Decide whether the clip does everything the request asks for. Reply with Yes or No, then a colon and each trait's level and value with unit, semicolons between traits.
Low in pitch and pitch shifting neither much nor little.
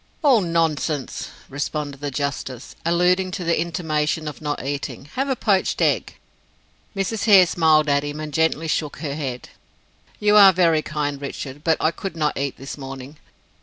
No: medium, 155 Hz; average, 3.3 semitones